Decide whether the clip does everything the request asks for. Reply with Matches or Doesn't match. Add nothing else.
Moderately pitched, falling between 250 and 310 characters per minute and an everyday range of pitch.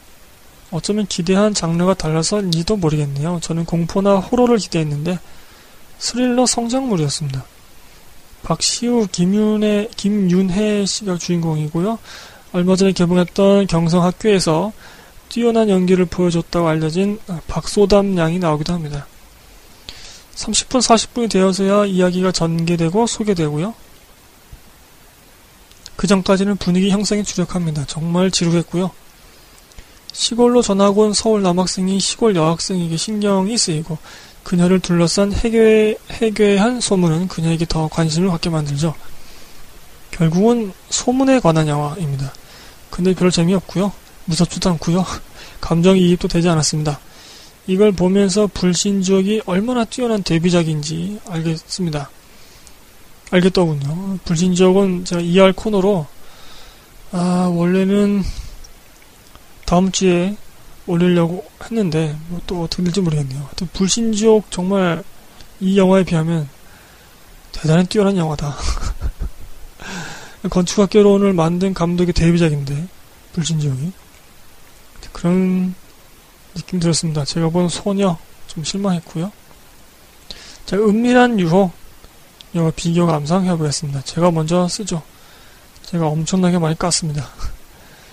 Matches